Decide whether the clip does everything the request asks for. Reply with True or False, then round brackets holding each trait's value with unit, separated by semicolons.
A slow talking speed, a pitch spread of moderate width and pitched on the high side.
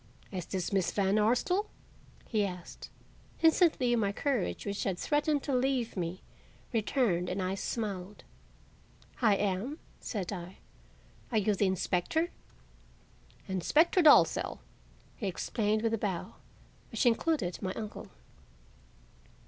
True (120 wpm; 5.0 semitones; 210 Hz)